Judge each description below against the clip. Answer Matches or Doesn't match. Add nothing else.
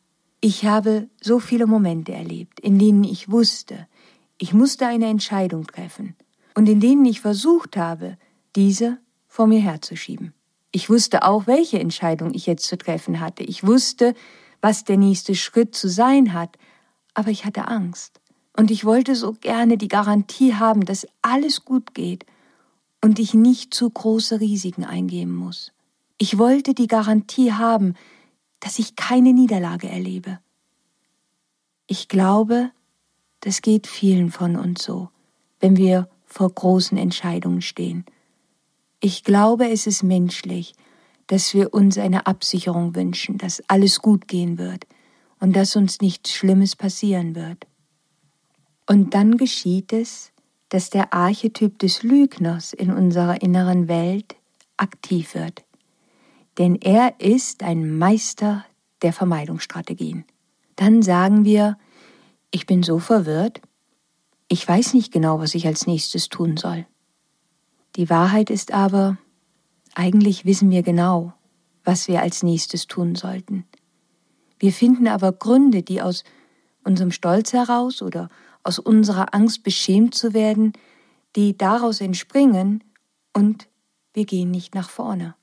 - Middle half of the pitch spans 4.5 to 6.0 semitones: Doesn't match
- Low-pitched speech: Doesn't match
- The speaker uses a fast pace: Doesn't match